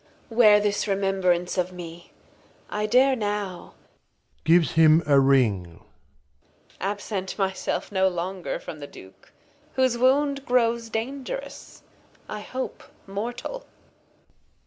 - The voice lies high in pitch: Yes, high, 200 Hz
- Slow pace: Yes, slow, 110 wpm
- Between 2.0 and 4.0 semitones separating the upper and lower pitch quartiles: No, average, 5.3 semitones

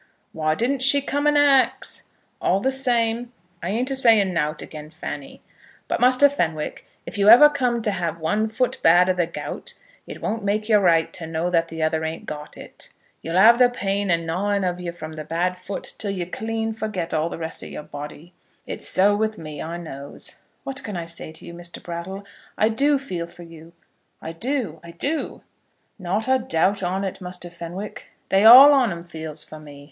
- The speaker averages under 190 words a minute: No, fast, 205 wpm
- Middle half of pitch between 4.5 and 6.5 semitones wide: Yes, wide, 5.4 semitones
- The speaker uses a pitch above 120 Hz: Yes, medium, 185 Hz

